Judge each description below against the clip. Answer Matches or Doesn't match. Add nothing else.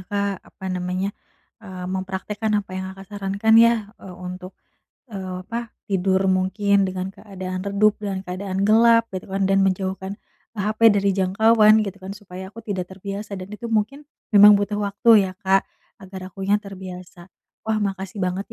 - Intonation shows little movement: Matches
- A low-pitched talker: Doesn't match